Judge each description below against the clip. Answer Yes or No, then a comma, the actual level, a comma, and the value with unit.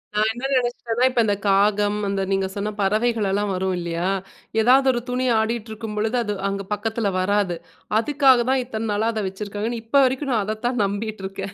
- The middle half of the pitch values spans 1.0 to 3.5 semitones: Yes, average, 3.1 semitones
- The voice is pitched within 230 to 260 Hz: No, high, 215 Hz